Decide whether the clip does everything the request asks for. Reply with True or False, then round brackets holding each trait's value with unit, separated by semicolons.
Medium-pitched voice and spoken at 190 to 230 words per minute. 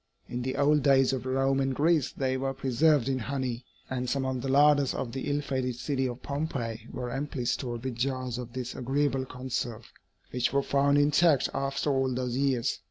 False (130 Hz; 195 wpm)